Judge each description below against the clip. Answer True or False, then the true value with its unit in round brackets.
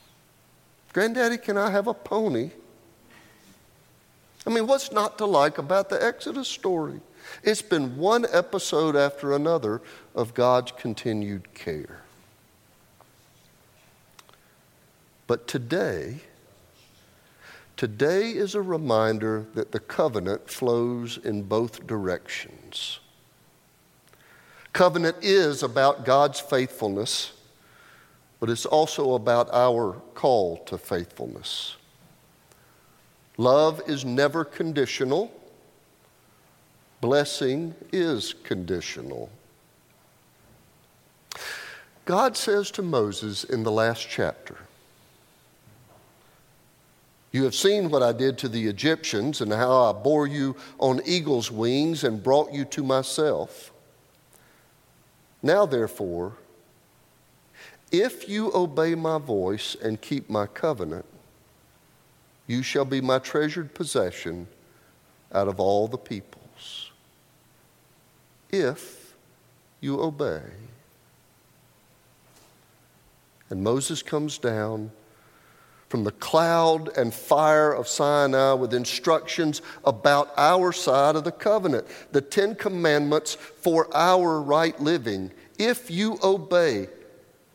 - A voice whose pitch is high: False (140 Hz)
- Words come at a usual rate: False (100 wpm)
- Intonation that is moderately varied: False (5.8 semitones)